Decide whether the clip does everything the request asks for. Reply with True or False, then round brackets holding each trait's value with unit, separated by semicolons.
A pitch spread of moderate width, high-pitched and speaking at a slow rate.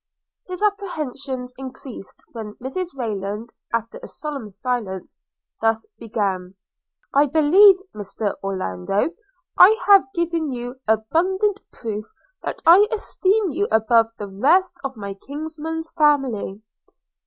False (7.8 semitones; 260 Hz; 115 wpm)